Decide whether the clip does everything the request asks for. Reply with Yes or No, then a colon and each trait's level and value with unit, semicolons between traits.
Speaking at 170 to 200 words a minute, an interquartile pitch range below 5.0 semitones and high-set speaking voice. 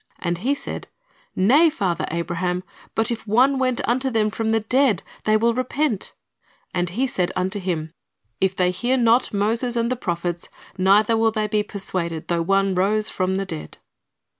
Yes: average, 175 wpm; average, 4.4 semitones; high, 210 Hz